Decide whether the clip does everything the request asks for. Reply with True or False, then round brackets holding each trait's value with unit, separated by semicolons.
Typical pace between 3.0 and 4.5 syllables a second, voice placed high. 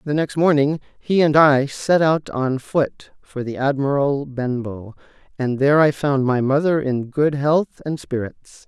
False (4.1 syllables/s; 140 Hz)